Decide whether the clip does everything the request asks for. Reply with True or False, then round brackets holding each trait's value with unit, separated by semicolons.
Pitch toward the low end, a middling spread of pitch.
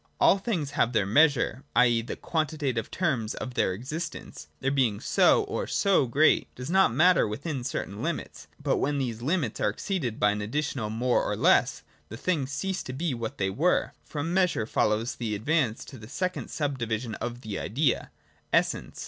False (130 Hz; 5.7 semitones)